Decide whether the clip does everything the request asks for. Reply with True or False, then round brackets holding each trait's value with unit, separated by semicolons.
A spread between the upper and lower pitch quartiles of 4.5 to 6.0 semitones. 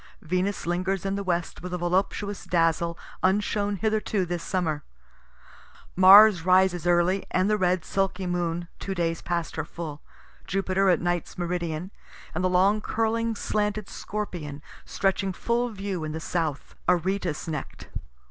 False (2.4 semitones)